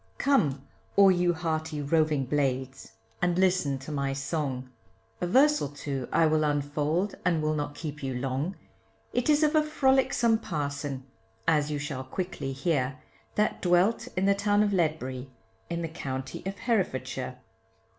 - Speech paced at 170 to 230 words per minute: No, average, 155 wpm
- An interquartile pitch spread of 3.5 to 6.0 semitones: Yes, average, 5.2 semitones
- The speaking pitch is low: No, medium, 155 Hz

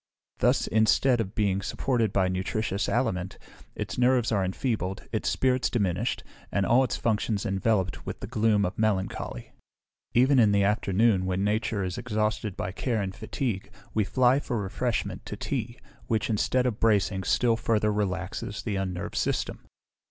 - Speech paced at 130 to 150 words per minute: No, average, 160 wpm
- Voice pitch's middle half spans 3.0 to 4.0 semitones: Yes, average, 3.3 semitones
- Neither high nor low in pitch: No, low, 105 Hz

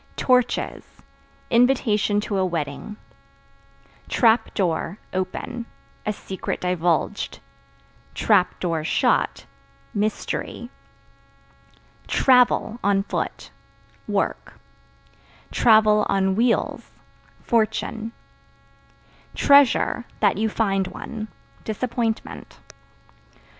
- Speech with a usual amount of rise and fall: Yes, average, 3.3 semitones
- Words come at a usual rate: No, slow, 65 wpm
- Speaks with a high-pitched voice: Yes, high, 215 Hz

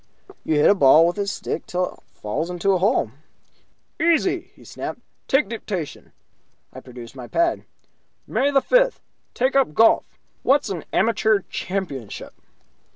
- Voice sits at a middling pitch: No, high, 195 Hz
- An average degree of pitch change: No, wide, 8.8 semitones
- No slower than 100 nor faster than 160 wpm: Yes, average, 150 wpm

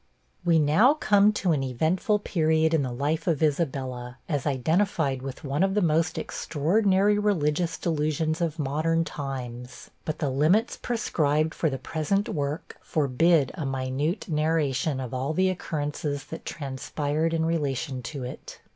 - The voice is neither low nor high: Yes, medium, 155 Hz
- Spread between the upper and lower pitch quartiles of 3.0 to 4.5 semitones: Yes, average, 3.5 semitones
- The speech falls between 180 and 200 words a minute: No, average, 150 wpm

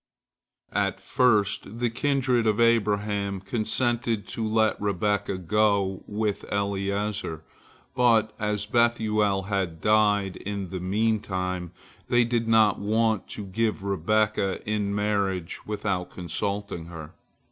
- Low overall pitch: Yes, low, 105 Hz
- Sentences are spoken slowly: Yes, slow, 115 wpm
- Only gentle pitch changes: Yes, narrow, 2.0 semitones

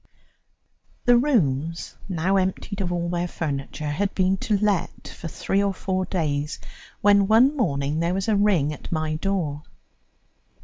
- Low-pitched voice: No, medium, 185 Hz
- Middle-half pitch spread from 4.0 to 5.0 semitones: Yes, average, 4.4 semitones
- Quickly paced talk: No, average, 150 wpm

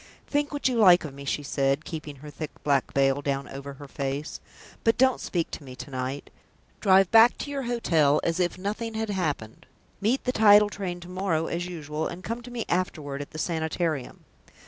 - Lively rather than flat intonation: Yes, wide, 6.4 semitones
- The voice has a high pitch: No, medium, 170 Hz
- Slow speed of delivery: No, fast, 205 wpm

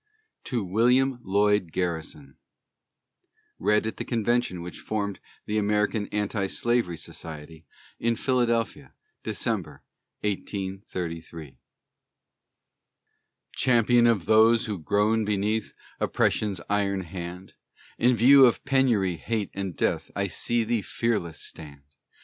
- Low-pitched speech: Yes, low, 105 Hz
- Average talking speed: No, slow, 110 wpm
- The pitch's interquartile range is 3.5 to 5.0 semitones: Yes, average, 4.3 semitones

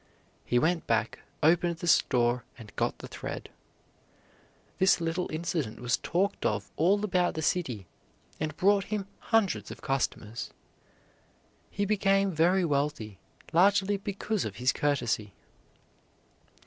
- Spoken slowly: Yes, slow, 125 wpm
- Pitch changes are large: Yes, wide, 7.4 semitones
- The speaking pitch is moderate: Yes, medium, 165 Hz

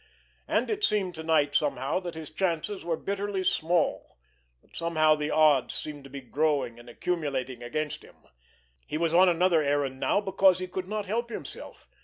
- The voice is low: No, medium, 160 Hz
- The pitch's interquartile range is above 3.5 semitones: Yes, average, 4.3 semitones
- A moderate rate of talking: Yes, average, 180 wpm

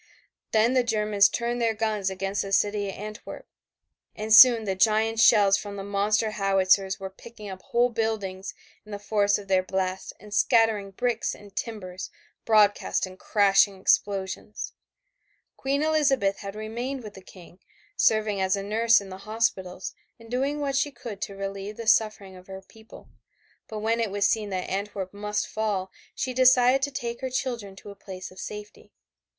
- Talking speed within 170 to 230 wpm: Yes, average, 175 wpm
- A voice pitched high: Yes, high, 210 Hz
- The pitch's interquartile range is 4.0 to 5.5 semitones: No, average, 2.7 semitones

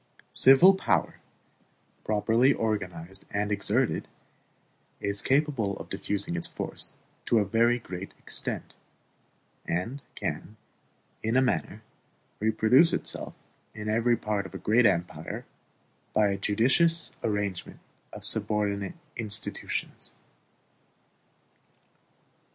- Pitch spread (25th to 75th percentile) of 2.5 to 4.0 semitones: Yes, average, 3.3 semitones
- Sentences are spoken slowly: Yes, slow, 100 wpm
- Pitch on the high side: No, low, 110 Hz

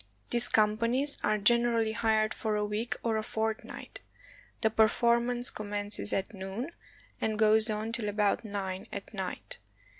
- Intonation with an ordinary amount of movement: No, narrow, 2.0 semitones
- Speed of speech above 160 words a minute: No, average, 145 wpm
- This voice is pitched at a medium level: No, high, 220 Hz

